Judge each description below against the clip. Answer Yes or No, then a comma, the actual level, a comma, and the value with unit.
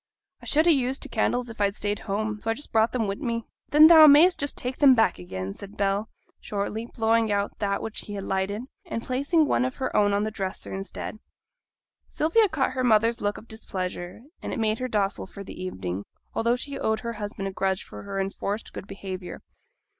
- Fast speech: Yes, fast, 220 wpm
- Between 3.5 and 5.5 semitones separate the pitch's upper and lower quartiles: Yes, average, 4.0 semitones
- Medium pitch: No, high, 220 Hz